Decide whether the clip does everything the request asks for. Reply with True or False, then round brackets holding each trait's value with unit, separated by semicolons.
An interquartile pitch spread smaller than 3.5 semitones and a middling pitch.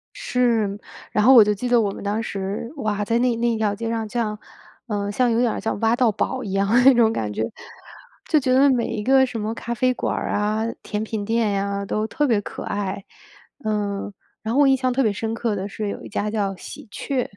False (2.9 semitones; 220 Hz)